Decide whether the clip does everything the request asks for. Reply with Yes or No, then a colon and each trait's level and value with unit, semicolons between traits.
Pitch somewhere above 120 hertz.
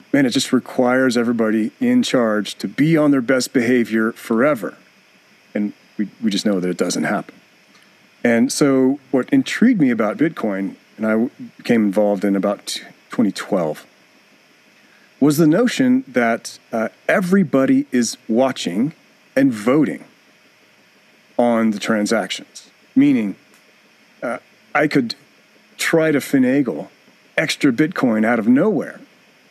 Yes: low, 135 Hz